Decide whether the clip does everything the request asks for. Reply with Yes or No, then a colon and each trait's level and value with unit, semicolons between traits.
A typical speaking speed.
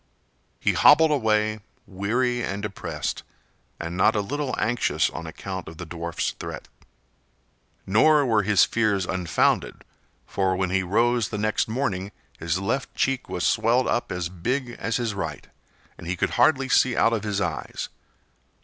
Yes: average, 155 wpm